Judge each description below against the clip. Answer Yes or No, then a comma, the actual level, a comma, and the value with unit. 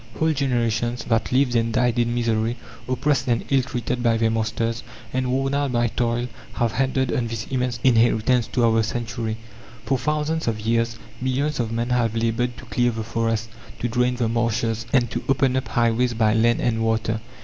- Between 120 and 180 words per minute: No, average, 190 wpm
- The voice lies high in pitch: No, low, 120 Hz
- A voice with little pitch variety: Yes, narrow, 1.9 semitones